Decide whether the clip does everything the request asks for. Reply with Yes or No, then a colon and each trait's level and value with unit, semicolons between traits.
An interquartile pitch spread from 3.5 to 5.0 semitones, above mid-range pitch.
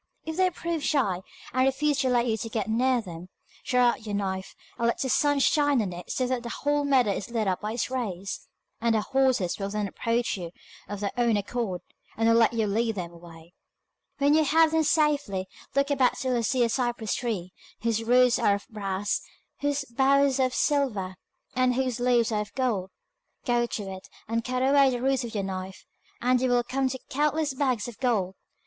Yes: average, 4.5 semitones; high, 240 Hz